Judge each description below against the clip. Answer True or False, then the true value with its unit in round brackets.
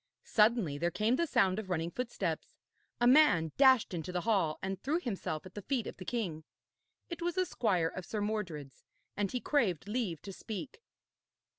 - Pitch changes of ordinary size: False (5.9 semitones)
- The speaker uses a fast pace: False (185 wpm)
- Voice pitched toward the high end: True (205 Hz)